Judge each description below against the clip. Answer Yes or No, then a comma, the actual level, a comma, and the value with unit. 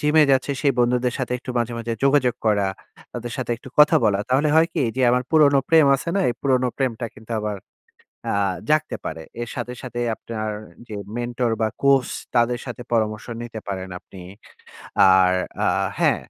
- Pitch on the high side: No, low, 120 Hz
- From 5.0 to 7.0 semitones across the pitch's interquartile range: No, average, 3.3 semitones